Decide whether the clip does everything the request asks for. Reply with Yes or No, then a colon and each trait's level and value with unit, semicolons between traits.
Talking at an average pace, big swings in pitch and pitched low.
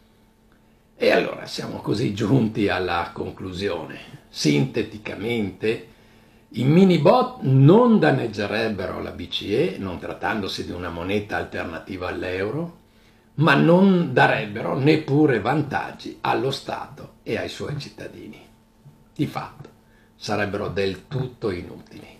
No: slow, 105 wpm; wide, 6.5 semitones; low, 110 Hz